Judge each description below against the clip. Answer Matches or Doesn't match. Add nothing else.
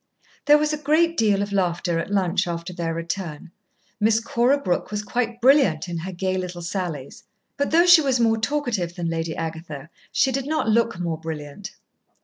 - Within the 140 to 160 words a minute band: Doesn't match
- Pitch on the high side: Matches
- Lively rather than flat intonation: Matches